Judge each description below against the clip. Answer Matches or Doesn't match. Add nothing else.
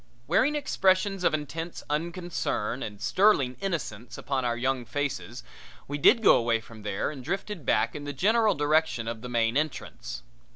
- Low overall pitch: Doesn't match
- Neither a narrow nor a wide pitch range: Doesn't match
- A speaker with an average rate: Matches